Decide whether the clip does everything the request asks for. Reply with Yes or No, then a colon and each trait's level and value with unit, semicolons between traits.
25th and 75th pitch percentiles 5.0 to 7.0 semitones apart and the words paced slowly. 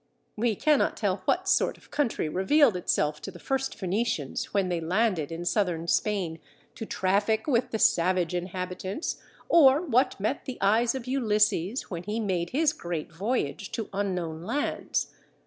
No: wide, 5.4 semitones; average, 160 wpm